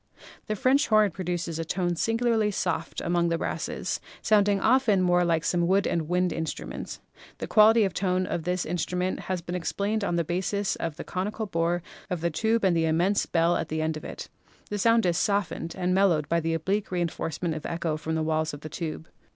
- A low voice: No, medium, 175 Hz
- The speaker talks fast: Yes, fast, 210 wpm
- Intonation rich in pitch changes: No, average, 3.3 semitones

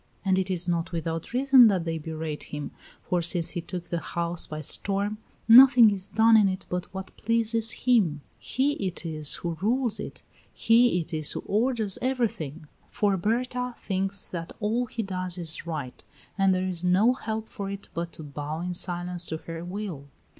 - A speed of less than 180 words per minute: No, average, 185 wpm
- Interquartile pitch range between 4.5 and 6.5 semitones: Yes, average, 4.8 semitones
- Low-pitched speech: No, medium, 185 Hz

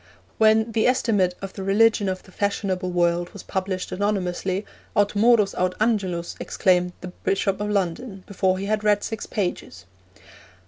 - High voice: Yes, high, 195 Hz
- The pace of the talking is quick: No, average, 155 wpm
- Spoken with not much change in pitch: Yes, narrow, 2.3 semitones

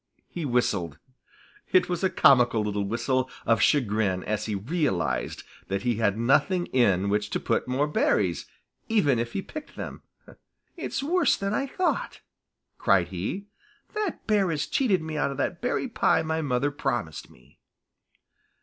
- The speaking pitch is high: No, low, 130 Hz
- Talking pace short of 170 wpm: Yes, average, 160 wpm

